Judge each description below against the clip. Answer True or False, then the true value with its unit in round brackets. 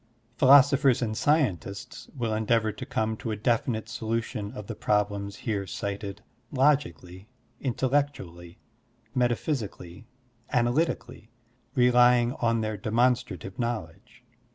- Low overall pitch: True (115 Hz)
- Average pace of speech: False (105 wpm)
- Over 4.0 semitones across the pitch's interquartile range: False (3.3 semitones)